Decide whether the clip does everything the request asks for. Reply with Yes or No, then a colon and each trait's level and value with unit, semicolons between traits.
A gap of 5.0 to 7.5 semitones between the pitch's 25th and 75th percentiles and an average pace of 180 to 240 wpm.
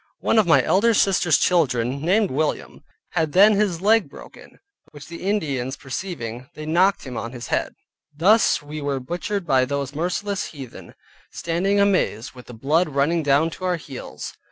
No: wide, 5.6 semitones; average, 170 wpm